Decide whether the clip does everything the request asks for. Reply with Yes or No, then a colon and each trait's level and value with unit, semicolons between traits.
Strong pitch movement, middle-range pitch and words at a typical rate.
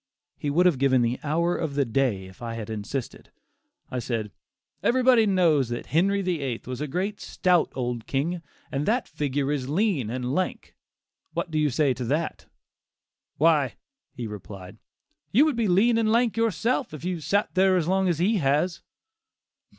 Yes: wide, 6.6 semitones; medium, 150 Hz; average, 175 wpm